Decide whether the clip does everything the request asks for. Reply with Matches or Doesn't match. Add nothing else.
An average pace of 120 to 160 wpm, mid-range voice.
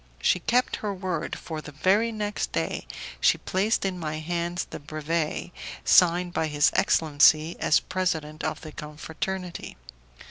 Matches